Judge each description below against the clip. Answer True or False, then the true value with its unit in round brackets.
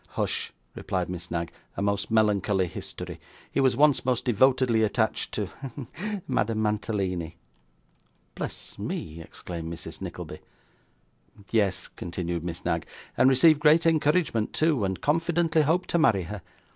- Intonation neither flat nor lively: False (8.1 semitones)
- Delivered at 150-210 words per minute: False (140 wpm)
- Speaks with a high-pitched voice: False (110 Hz)